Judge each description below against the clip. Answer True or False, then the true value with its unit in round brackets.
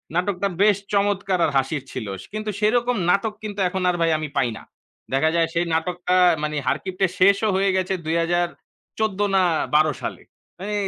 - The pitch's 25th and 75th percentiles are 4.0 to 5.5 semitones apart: False (3.4 semitones)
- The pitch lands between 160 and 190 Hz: True (185 Hz)